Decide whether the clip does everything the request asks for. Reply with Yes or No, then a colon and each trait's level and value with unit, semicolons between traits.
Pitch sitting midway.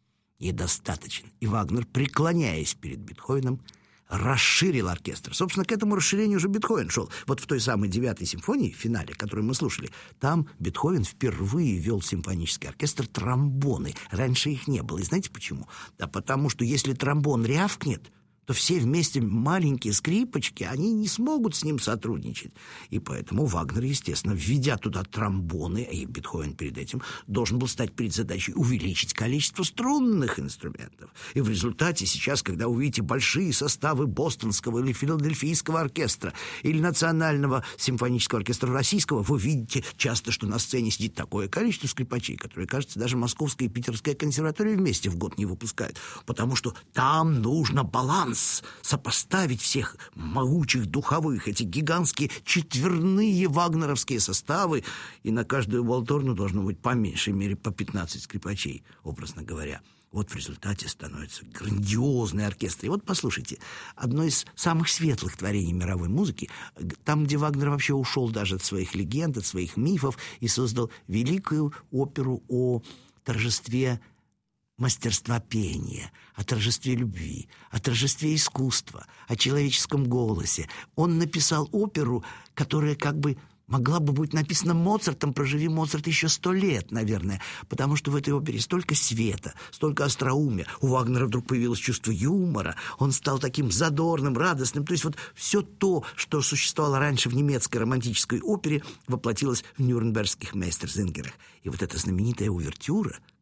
No: low, 125 Hz